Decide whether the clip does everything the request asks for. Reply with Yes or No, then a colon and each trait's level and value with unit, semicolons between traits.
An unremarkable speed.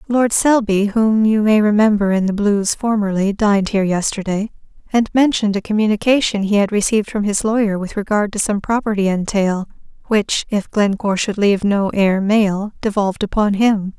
Yes: average, 170 wpm